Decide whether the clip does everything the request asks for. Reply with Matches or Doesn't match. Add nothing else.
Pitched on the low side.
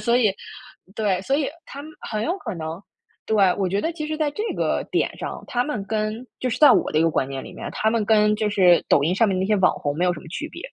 Doesn't match